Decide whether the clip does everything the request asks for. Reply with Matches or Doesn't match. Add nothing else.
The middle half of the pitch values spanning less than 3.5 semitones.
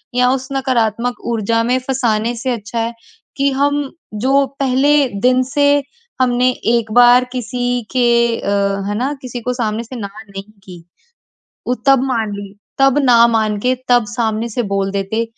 Matches